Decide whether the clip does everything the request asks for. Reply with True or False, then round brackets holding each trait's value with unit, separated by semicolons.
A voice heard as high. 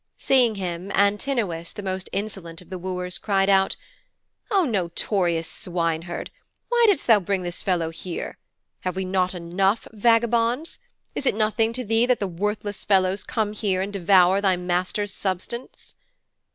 True (195 Hz)